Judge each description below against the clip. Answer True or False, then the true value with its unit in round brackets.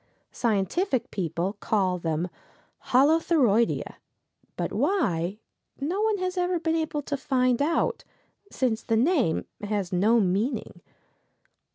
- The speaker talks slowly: True (110 wpm)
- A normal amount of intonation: False (8.5 semitones)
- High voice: True (245 Hz)